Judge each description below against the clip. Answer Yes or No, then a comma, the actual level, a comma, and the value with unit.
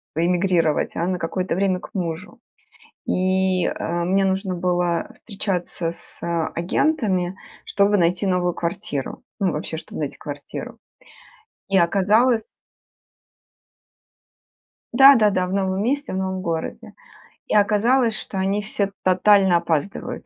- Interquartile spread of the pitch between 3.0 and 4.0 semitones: No, narrow, 2.5 semitones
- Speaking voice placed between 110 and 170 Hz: No, medium, 185 Hz